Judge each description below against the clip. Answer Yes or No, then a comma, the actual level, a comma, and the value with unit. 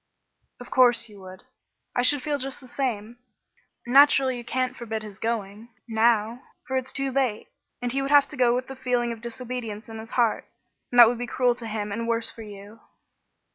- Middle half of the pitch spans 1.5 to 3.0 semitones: Yes, narrow, 2.5 semitones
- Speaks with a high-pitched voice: Yes, high, 240 Hz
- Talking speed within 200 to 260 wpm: Yes, fast, 205 wpm